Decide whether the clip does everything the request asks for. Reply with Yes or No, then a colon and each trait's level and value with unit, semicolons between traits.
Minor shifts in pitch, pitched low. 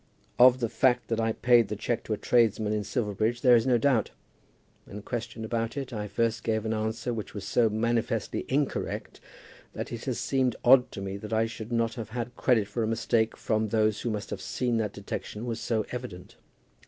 Yes: narrow, 1.9 semitones; low, 115 Hz